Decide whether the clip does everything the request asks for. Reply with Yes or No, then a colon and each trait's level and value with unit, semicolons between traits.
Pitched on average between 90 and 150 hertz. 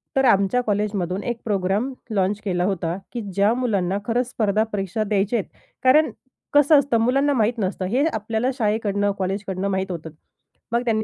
No: high, 210 Hz